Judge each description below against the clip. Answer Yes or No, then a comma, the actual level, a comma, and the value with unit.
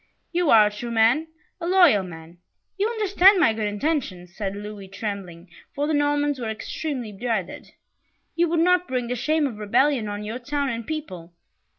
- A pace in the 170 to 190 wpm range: Yes, average, 180 wpm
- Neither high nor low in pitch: No, high, 240 Hz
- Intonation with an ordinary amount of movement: No, wide, 6.9 semitones